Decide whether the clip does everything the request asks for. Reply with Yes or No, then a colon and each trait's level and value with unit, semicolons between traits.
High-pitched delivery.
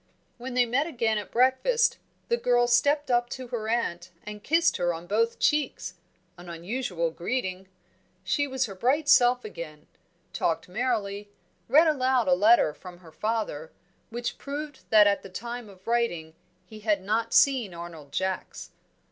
Yes: high, 230 Hz